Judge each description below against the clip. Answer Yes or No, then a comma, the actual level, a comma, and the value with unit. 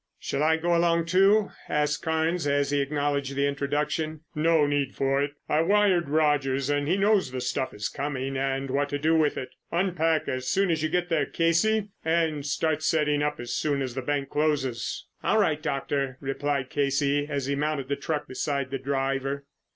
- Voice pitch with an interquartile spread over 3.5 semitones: No, average, 2.7 semitones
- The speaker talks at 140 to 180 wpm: No, average, 190 wpm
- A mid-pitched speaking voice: Yes, medium, 145 Hz